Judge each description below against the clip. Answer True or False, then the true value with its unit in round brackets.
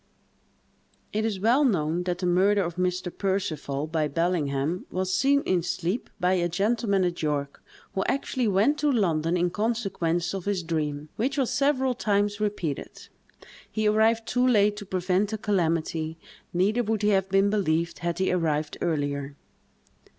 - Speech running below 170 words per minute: True (160 wpm)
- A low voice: False (185 Hz)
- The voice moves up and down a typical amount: True (4.1 semitones)